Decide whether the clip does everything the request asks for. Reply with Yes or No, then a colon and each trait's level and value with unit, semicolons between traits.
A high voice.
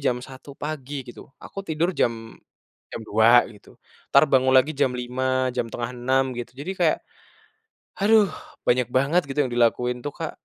No: low, 130 Hz